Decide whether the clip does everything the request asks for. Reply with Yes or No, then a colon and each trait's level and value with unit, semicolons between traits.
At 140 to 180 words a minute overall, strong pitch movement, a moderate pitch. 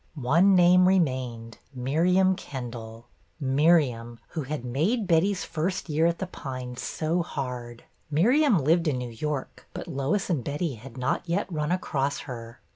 Yes: average, 150 wpm; wide, 5.7 semitones; medium, 150 Hz